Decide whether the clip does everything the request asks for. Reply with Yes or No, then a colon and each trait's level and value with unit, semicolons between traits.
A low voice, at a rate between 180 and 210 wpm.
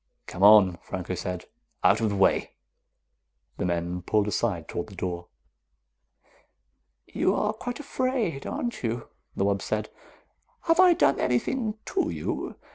No: low, 105 Hz; average, 140 wpm